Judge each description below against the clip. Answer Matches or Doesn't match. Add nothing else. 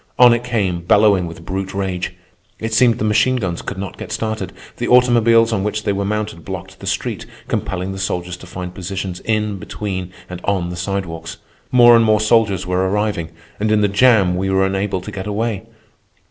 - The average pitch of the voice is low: Matches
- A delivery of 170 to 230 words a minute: Matches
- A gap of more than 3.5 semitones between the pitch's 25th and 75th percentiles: Doesn't match